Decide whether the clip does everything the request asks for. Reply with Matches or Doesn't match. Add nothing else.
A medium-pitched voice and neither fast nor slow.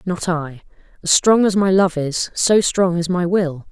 Doesn't match